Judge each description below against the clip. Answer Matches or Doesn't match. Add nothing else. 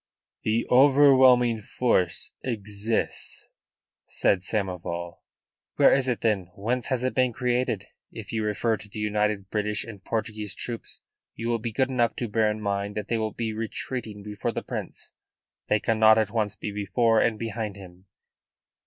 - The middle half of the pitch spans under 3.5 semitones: Matches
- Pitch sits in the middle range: Doesn't match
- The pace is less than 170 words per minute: Matches